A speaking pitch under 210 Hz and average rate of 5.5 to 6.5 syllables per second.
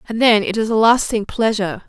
No: high, 220 Hz; 5.9 syllables/s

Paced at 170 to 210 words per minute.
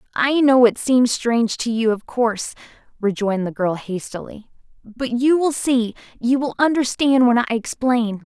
No: average, 160 wpm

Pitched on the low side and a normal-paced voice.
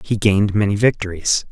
Yes: low, 105 Hz; average, 160 wpm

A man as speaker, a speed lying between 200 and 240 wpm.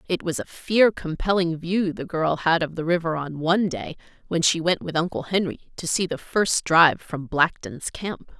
No: female; fast, 205 wpm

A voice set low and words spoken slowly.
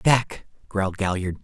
Yes: low, 100 Hz; slow, 125 wpm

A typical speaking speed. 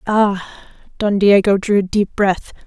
Yes: average, 155 wpm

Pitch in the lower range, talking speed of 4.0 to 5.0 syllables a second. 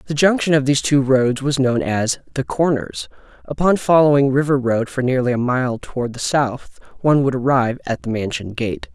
No: low, 130 Hz; 5.3 syllables/s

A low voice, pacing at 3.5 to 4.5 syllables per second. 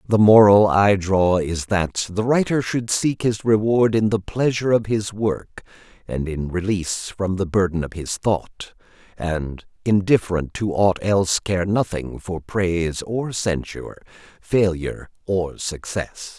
Yes: low, 100 Hz; 4.1 syllables/s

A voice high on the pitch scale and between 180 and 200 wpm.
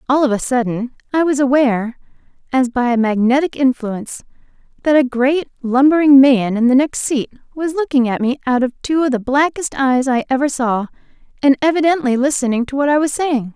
Yes: very high, 265 Hz; average, 190 wpm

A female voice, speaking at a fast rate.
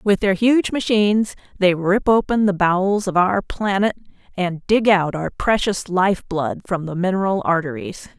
No: female; average, 170 wpm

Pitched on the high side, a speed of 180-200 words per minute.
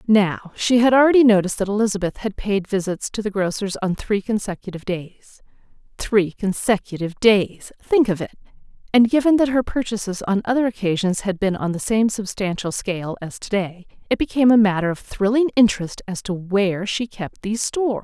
Yes: high, 205 Hz; average, 185 wpm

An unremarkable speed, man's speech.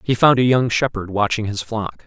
No: fast, 235 wpm; male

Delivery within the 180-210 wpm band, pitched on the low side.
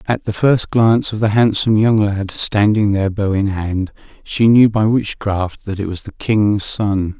Yes: average, 200 wpm; low, 105 Hz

